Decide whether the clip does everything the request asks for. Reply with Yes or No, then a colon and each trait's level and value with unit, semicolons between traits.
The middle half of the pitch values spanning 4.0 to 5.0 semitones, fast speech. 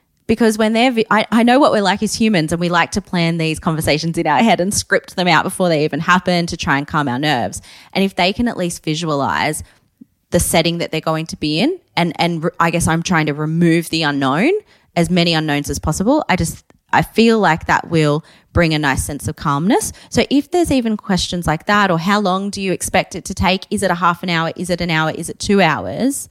Yes: average, 4.5 semitones; fast, 250 wpm